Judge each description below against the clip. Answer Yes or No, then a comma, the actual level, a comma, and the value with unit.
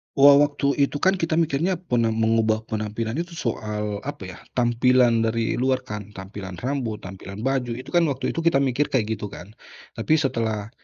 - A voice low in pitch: Yes, low, 120 Hz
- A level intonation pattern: No, average, 4.6 semitones